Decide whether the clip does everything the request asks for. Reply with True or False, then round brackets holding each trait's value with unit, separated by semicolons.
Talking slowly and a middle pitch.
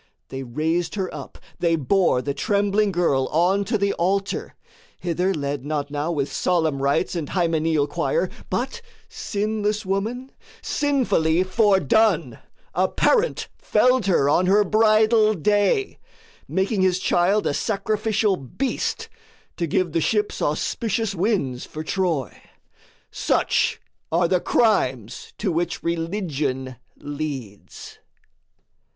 True (120 wpm; 180 Hz)